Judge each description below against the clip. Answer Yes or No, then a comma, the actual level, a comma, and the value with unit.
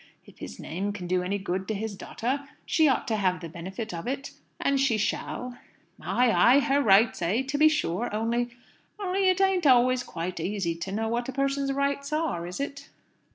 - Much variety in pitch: Yes, wide, 6.4 semitones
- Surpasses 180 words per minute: Yes, average, 200 wpm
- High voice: Yes, high, 240 Hz